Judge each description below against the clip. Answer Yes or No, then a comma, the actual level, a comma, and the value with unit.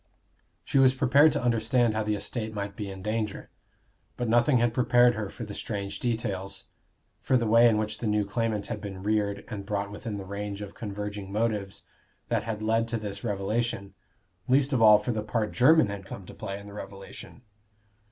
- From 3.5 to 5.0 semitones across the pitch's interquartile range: No, narrow, 2.6 semitones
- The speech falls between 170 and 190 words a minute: No, average, 200 wpm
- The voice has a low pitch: Yes, low, 105 Hz